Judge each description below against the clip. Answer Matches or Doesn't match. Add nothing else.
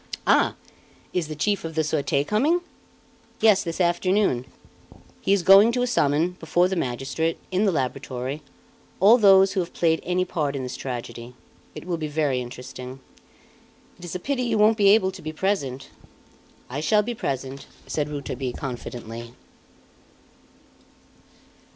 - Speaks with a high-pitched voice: Doesn't match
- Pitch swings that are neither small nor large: Doesn't match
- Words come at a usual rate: Matches